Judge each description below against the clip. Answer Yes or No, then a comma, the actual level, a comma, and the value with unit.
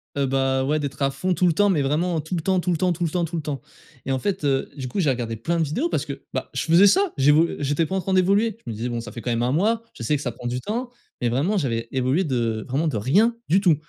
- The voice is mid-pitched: Yes, medium, 150 Hz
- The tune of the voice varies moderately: No, wide, 5.8 semitones